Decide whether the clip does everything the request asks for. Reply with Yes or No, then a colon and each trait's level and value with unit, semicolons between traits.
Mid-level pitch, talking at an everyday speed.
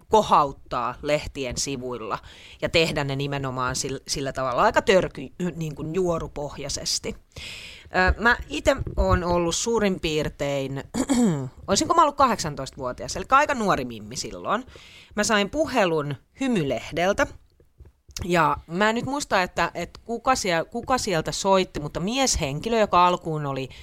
Yes: medium, 160 Hz; average, 130 wpm